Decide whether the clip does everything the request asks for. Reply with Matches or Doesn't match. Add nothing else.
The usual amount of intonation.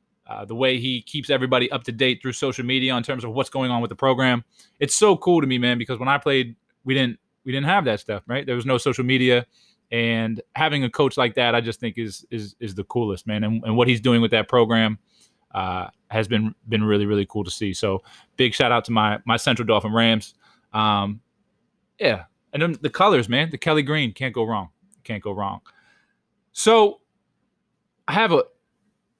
Matches